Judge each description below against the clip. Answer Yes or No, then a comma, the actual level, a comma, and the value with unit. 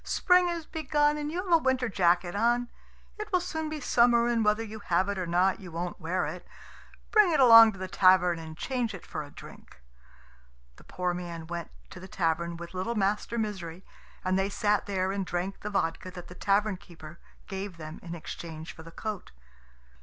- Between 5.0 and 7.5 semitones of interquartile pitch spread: Yes, average, 5.3 semitones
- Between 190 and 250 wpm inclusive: Yes, fast, 205 wpm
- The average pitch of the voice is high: Yes, high, 195 Hz